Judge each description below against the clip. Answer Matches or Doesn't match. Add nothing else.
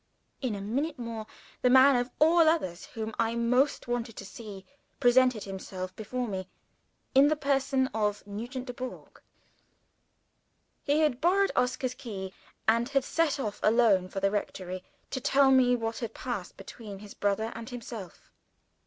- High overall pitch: Matches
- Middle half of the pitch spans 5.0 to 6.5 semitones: Doesn't match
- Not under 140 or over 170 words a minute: Matches